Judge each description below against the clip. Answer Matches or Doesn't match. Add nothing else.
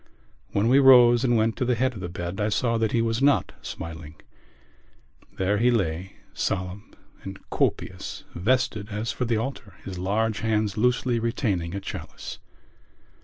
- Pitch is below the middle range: Matches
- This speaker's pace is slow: Doesn't match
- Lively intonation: Doesn't match